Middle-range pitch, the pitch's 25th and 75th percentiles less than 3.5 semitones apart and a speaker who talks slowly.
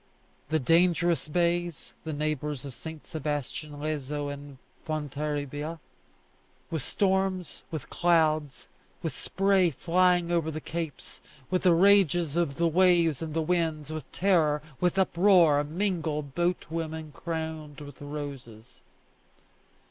Yes: medium, 160 Hz; average, 2.8 semitones; slow, 120 wpm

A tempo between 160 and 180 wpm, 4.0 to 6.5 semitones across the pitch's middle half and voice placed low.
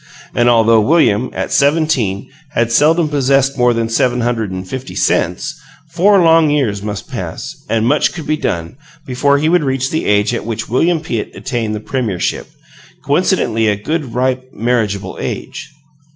Yes: average, 165 wpm; average, 5.1 semitones; low, 125 Hz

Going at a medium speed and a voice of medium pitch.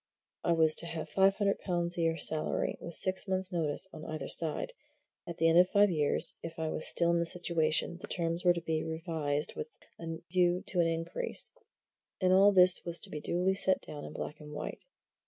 No: fast, 215 wpm; medium, 170 Hz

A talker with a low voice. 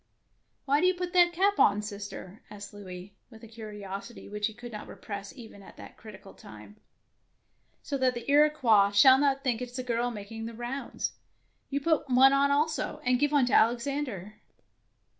No: high, 240 Hz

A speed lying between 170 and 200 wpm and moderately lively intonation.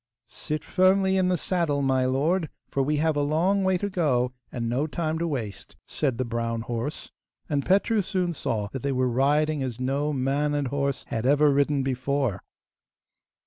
Yes: average, 185 wpm; average, 3.9 semitones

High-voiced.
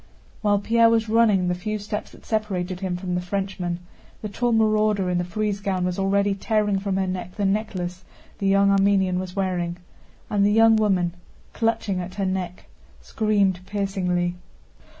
Yes: high, 195 Hz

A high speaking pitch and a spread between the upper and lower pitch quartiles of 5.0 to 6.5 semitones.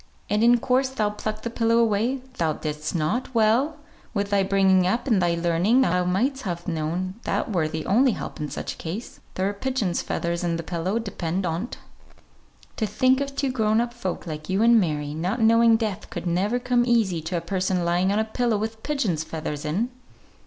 Yes: high, 200 Hz; average, 5.3 semitones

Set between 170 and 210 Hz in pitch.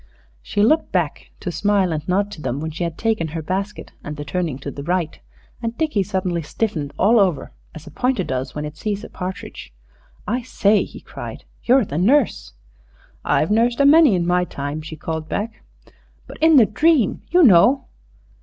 Yes: medium, 185 Hz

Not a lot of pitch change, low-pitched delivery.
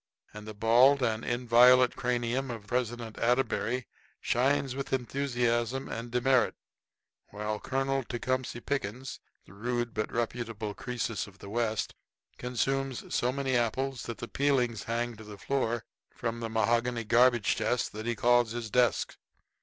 Yes: narrow, 1.9 semitones; low, 120 Hz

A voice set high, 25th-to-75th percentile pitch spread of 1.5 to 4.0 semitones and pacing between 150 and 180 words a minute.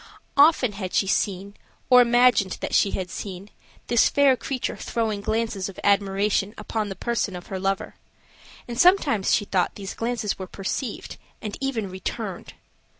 Yes: high, 210 Hz; average, 3.6 semitones; average, 155 wpm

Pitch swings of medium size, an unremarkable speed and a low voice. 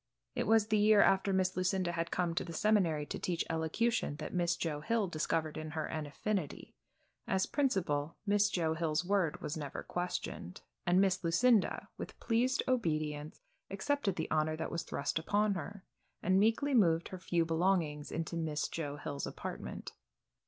No: average, 4.3 semitones; average, 170 wpm; medium, 175 Hz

